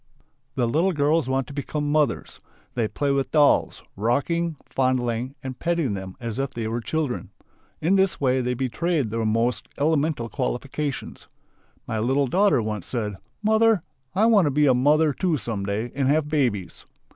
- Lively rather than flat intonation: No, average, 4.7 semitones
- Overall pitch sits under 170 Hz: Yes, low, 135 Hz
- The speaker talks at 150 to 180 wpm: Yes, average, 170 wpm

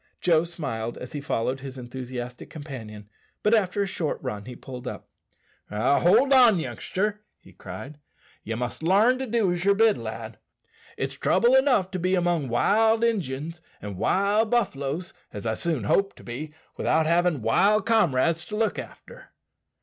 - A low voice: No, medium, 170 Hz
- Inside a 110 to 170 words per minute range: Yes, average, 165 wpm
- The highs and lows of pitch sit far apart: Yes, wide, 8.3 semitones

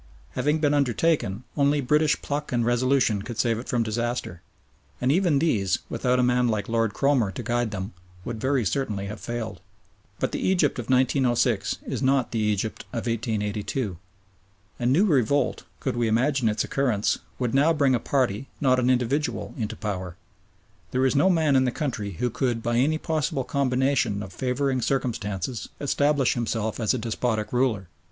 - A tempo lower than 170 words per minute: No, average, 175 wpm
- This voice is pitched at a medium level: No, low, 125 Hz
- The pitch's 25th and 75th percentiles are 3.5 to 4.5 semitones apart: Yes, average, 3.8 semitones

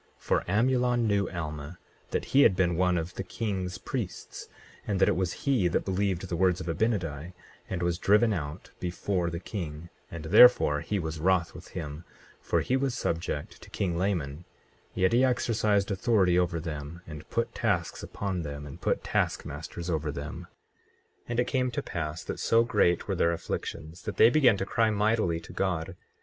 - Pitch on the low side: Yes, very low, 90 Hz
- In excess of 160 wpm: Yes, average, 190 wpm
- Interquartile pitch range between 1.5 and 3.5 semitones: No, average, 4.2 semitones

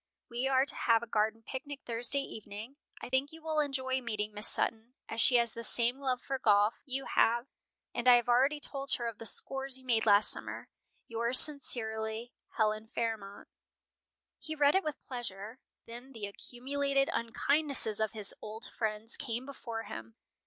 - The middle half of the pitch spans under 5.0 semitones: Yes, average, 3.5 semitones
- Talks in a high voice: Yes, high, 240 Hz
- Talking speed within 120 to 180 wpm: Yes, average, 175 wpm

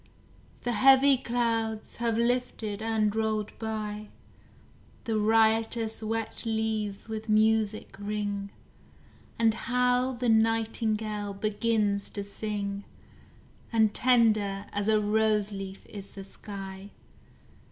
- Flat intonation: Yes, narrow, 1.6 semitones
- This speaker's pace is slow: Yes, slow, 105 wpm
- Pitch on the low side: No, high, 220 Hz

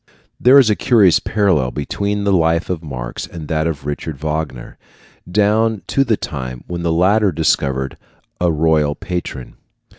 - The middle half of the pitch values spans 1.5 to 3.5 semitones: No, wide, 5.4 semitones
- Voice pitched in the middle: No, very low, 85 Hz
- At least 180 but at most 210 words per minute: No, average, 155 wpm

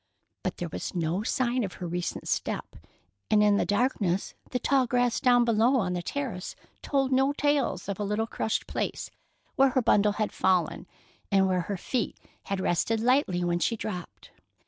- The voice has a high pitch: Yes, high, 210 Hz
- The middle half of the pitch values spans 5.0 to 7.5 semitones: Yes, wide, 5.4 semitones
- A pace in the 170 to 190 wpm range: Yes, average, 180 wpm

